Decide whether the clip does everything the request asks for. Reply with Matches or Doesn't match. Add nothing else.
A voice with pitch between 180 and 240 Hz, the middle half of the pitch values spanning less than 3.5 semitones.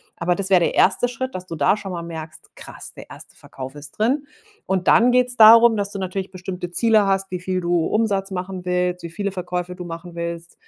Matches